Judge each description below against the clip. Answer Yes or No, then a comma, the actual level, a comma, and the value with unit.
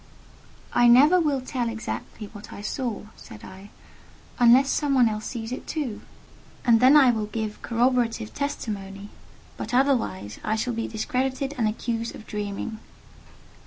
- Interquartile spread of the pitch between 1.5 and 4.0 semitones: Yes, average, 3.3 semitones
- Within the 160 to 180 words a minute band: No, average, 150 wpm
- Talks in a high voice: Yes, high, 235 Hz